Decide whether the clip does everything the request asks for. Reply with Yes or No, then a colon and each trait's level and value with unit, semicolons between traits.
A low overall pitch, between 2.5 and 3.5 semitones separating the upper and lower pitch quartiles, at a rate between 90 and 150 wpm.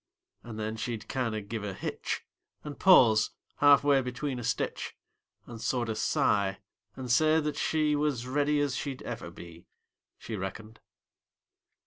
No: low, 125 Hz; average, 4.9 semitones; average, 145 wpm